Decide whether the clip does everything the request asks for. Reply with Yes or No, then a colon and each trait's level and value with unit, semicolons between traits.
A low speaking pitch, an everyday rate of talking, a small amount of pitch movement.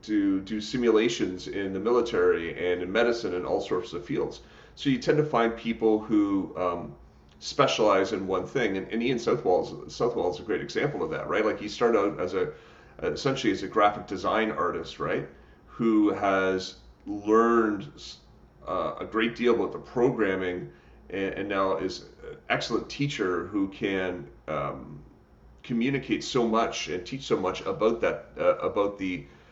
No: low, 105 Hz; average, 170 wpm; average, 4.0 semitones